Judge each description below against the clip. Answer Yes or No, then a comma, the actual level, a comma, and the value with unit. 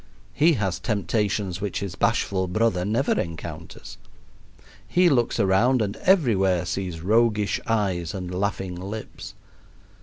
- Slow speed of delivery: Yes, slow, 120 wpm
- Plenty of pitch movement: No, average, 3.6 semitones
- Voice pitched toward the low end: Yes, low, 100 Hz